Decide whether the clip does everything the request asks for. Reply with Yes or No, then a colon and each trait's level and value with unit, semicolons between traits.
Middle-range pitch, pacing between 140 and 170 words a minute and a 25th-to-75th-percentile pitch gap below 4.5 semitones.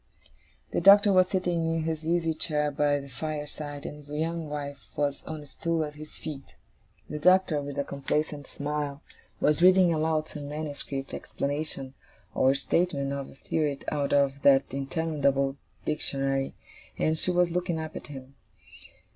Yes: medium, 150 Hz; average, 160 wpm; narrow, 2.5 semitones